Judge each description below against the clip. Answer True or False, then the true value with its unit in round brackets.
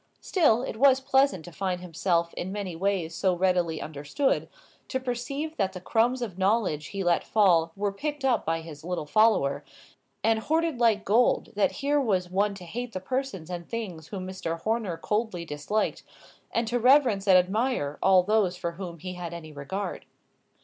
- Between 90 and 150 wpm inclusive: False (180 wpm)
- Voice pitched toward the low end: False (195 Hz)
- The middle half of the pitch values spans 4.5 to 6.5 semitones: True (5.1 semitones)